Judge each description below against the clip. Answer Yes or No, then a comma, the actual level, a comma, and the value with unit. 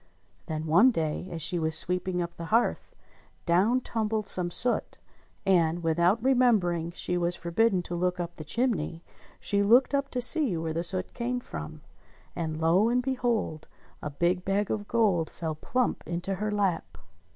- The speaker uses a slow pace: No, average, 170 wpm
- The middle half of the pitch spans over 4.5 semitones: Yes, average, 5.0 semitones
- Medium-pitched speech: Yes, medium, 180 Hz